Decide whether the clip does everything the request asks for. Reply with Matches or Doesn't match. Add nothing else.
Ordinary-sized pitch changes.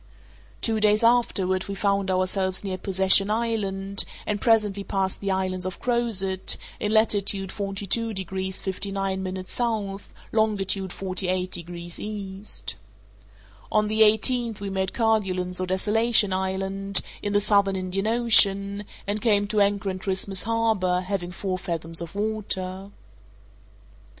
Doesn't match